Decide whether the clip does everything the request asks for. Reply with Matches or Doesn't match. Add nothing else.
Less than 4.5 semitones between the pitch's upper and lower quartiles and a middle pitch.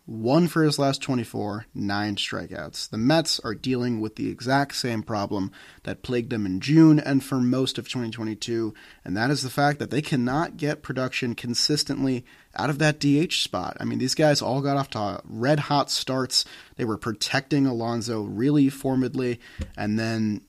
Doesn't match